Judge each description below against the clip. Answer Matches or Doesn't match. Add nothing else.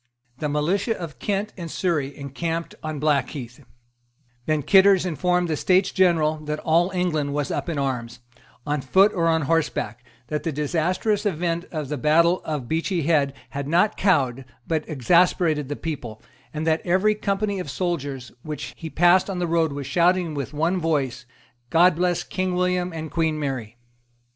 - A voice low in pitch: Doesn't match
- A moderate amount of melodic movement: Matches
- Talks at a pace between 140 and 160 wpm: Doesn't match